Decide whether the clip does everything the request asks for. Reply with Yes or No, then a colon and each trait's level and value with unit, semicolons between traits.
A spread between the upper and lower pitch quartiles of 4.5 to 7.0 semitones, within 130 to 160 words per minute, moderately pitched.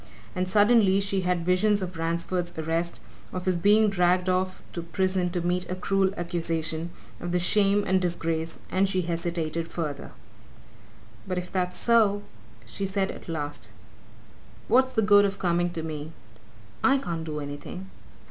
No: narrow, 2.6 semitones; average, 155 wpm; medium, 180 Hz